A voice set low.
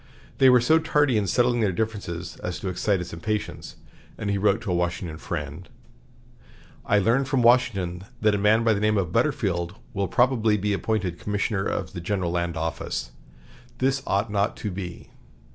Yes: low, 100 Hz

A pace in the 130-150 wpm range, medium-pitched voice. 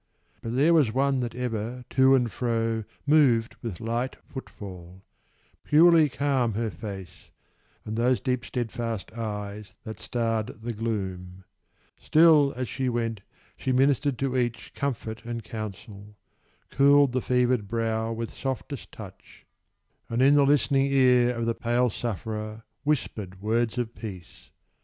No: average, 140 wpm; low, 115 Hz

